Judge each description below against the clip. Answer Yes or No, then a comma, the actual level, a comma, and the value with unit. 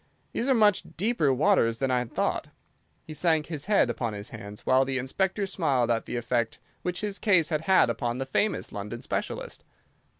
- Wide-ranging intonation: Yes, wide, 8.1 semitones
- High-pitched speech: No, low, 135 Hz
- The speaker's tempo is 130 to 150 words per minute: No, average, 195 wpm